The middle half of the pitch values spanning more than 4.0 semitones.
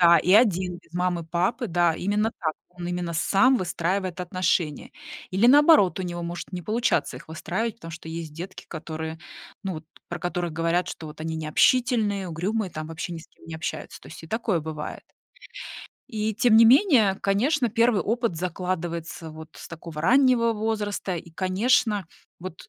Yes: average, 4.7 semitones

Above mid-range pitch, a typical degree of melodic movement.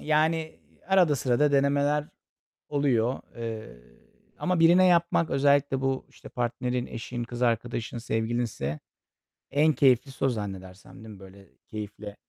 No: low, 125 Hz; average, 4.5 semitones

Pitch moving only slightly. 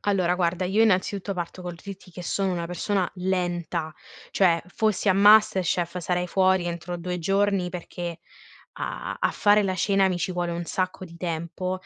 Yes: narrow, 1.8 semitones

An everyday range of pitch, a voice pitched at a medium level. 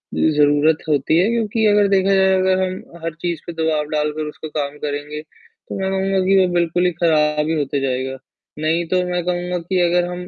Yes: average, 3.6 semitones; medium, 170 Hz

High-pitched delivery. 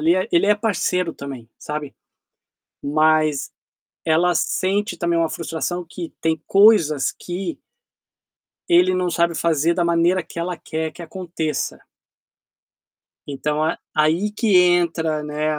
No: medium, 170 Hz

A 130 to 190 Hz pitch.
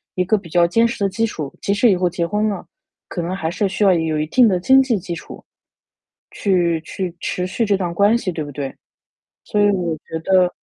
Yes: medium, 185 Hz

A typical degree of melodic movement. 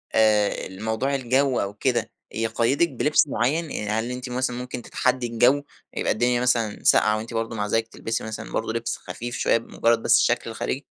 No: narrow, 2.2 semitones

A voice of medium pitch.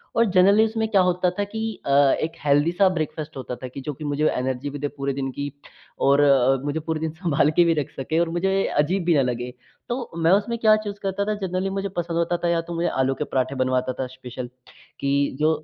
Yes: medium, 155 Hz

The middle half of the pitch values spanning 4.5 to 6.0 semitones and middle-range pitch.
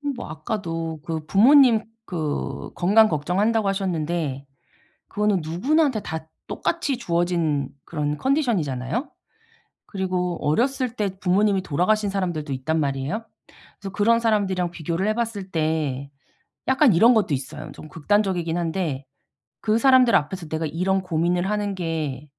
Yes: average, 5.2 semitones; medium, 180 Hz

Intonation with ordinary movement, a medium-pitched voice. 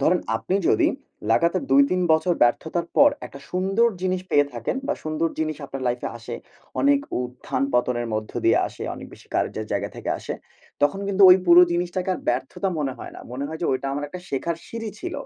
No: wide, 5.9 semitones; medium, 160 Hz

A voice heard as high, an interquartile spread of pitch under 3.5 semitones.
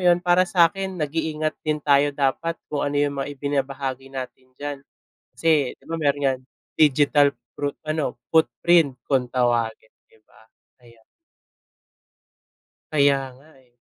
No: medium, 145 Hz; average, 2.8 semitones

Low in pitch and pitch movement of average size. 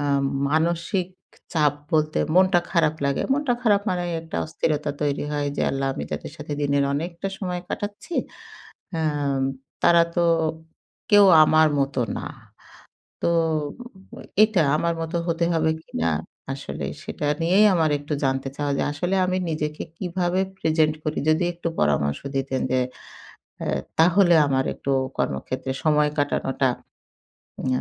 No: medium, 155 Hz; average, 3.6 semitones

